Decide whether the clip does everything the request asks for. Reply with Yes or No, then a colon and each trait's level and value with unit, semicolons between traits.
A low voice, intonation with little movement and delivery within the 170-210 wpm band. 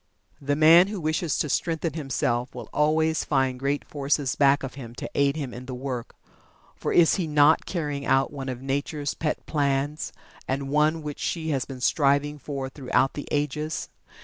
No: medium, 145 Hz; narrow, 2.3 semitones; average, 180 wpm